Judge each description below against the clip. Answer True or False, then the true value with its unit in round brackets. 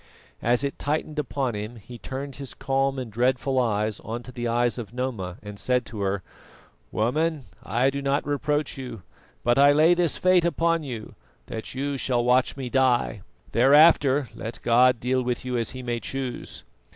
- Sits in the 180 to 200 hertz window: False (130 Hz)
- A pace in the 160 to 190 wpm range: True (180 wpm)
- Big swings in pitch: False (2.8 semitones)